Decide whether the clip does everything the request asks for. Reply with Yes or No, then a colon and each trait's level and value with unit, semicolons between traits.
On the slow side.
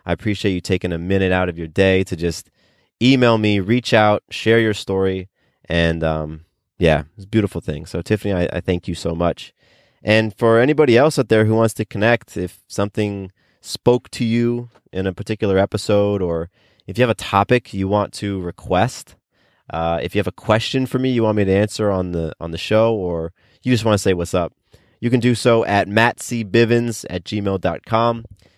No: fast, 205 wpm